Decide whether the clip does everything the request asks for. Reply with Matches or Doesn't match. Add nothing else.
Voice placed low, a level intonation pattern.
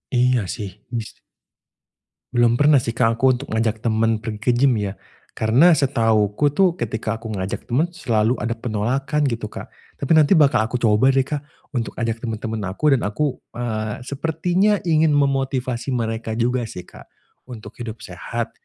Doesn't match